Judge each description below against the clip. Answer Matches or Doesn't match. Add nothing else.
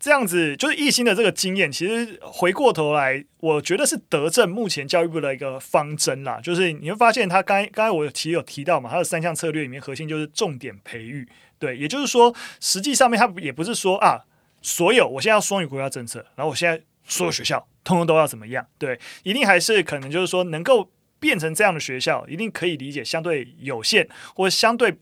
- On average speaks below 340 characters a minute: Doesn't match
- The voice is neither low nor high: Matches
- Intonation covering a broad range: Matches